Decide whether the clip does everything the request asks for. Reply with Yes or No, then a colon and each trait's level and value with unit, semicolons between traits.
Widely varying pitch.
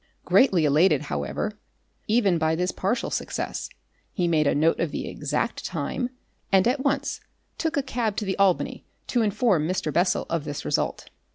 Yes: wide, 6.2 semitones